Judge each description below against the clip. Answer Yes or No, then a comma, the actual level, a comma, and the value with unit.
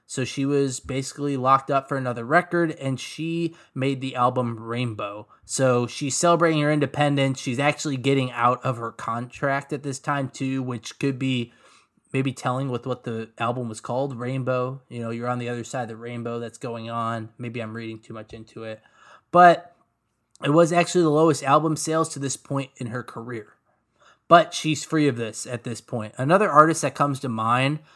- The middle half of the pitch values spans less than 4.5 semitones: Yes, average, 3.4 semitones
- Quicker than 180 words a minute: Yes, average, 195 wpm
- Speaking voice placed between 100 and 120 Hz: No, low, 130 Hz